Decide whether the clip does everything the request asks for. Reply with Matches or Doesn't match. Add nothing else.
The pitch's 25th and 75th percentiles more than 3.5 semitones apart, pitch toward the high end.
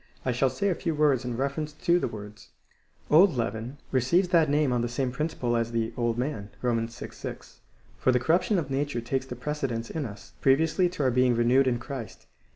Doesn't match